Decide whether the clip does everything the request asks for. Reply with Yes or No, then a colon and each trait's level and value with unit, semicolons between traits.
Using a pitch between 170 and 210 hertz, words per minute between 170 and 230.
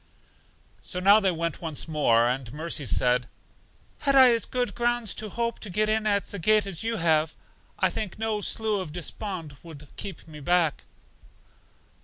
Yes: medium, 185 Hz; average, 180 wpm